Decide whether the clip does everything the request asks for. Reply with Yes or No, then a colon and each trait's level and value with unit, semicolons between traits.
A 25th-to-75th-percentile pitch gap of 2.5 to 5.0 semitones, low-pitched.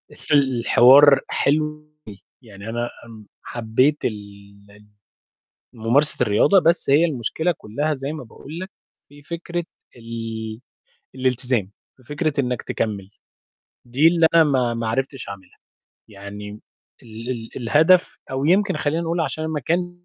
No: wide, 5.5 semitones; low, 130 Hz